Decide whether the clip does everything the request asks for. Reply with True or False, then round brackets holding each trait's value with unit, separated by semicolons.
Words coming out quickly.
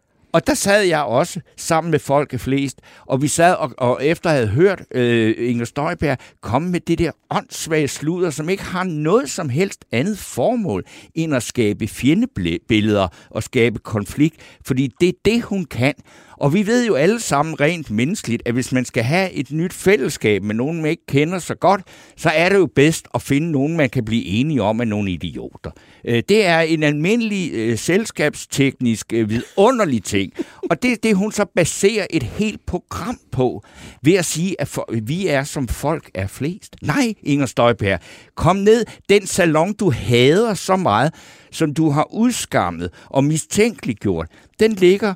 False (180 wpm)